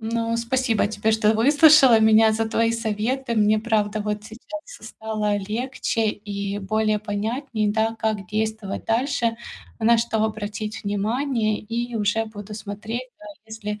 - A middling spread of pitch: No, narrow, 1.6 semitones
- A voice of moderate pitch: No, high, 220 Hz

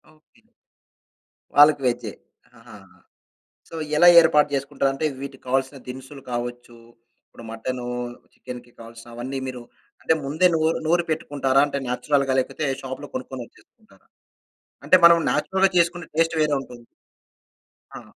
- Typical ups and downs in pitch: Yes, average, 3.7 semitones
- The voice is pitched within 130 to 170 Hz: Yes, low, 135 Hz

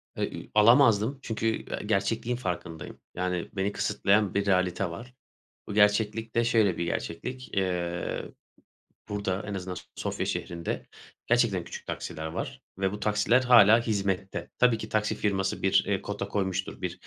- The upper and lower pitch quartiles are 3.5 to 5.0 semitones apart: No, average, 3.1 semitones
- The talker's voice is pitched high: No, low, 100 Hz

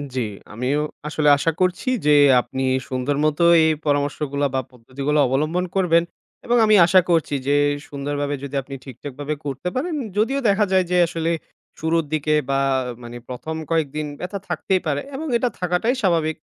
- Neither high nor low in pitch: Yes, medium, 155 Hz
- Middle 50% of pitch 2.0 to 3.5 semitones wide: No, average, 4.2 semitones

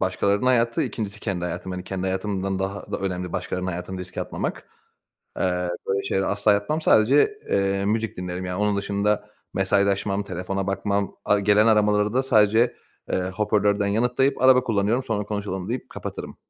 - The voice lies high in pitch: No, low, 100 Hz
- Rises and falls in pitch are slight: Yes, narrow, 2.1 semitones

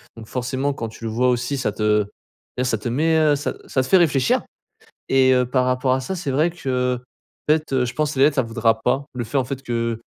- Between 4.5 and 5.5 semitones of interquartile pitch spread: No, average, 2.8 semitones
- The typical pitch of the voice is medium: No, low, 130 Hz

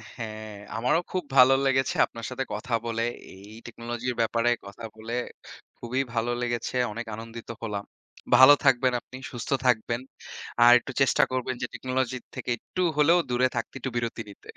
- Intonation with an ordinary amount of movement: No, narrow, 2.0 semitones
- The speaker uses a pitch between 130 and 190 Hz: No, low, 120 Hz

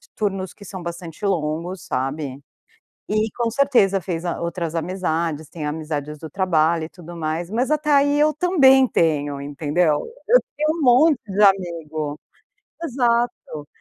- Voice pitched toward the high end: No, medium, 175 Hz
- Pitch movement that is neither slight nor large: No, wide, 6.9 semitones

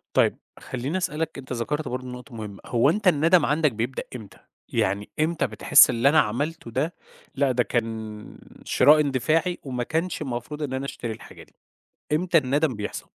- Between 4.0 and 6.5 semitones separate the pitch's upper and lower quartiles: Yes, average, 4.5 semitones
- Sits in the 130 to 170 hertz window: Yes, low, 135 Hz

